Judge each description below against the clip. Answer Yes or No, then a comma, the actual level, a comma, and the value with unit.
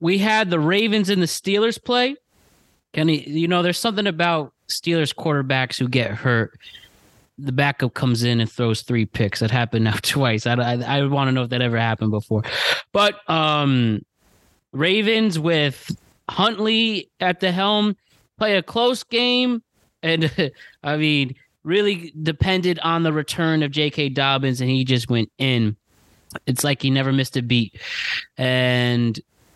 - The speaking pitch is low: No, medium, 145 Hz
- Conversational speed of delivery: Yes, average, 160 wpm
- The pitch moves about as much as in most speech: No, wide, 6.6 semitones